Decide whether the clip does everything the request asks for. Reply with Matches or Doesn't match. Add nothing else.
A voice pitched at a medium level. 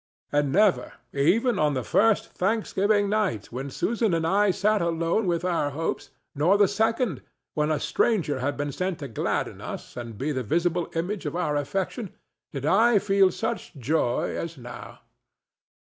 Matches